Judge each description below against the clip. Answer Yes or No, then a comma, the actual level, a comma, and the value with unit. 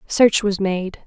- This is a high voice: Yes, high, 200 Hz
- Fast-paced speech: No, average, 170 wpm